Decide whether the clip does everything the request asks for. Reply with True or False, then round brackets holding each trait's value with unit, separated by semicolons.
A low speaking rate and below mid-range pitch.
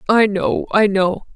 False (130 wpm; 200 Hz)